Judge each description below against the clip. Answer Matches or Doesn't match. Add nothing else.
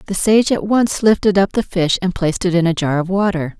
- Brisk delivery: Matches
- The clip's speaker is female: Matches